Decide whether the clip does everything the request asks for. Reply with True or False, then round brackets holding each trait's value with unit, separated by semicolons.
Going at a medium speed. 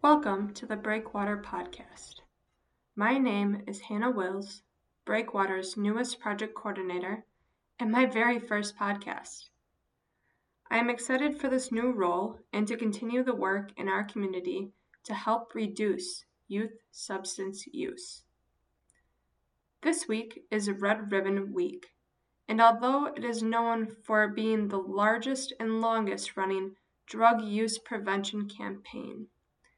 False (125 wpm)